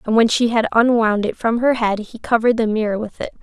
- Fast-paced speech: Yes, fast, 265 wpm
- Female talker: Yes, female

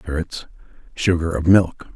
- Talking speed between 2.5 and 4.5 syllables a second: Yes, 4.4 syllables/s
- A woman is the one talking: No, male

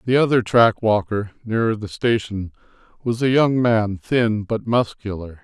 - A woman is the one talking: No, male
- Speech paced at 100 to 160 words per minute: Yes, average, 155 wpm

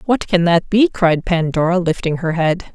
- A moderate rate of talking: Yes, average, 195 wpm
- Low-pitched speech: No, medium, 175 Hz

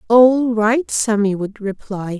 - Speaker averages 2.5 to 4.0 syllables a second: Yes, 3.5 syllables/s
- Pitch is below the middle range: No, high, 220 Hz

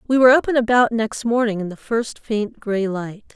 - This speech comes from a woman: Yes, female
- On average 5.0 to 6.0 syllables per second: Yes, 5.1 syllables/s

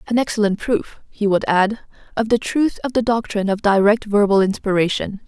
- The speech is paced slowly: No, average, 180 wpm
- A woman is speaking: Yes, female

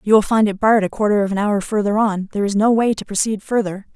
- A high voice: Yes, high, 210 Hz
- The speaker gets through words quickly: Yes, fast, 290 wpm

